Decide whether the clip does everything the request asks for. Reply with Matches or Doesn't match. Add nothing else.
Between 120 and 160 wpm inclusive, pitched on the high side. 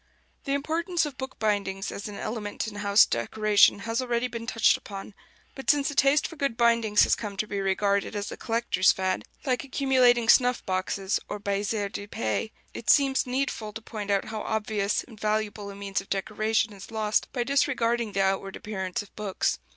Doesn't match